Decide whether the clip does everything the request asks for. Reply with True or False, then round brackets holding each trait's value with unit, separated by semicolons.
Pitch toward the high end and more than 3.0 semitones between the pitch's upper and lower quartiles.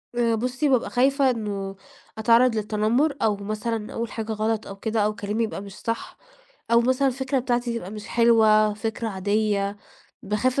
False (225 Hz; 2.4 semitones)